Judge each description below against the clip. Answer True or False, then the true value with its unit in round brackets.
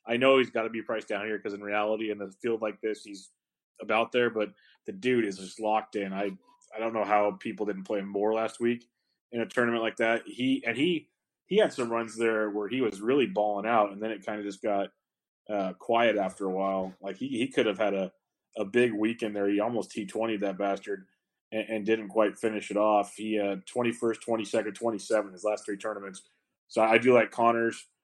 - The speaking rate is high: True (240 wpm)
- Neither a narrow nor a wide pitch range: False (2.1 semitones)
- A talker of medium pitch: False (110 Hz)